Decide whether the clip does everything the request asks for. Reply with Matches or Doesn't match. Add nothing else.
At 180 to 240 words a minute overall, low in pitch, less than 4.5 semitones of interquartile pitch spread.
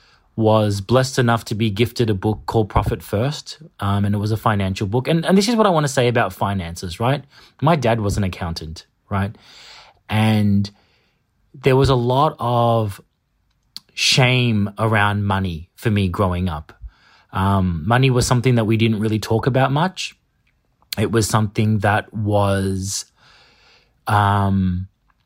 Doesn't match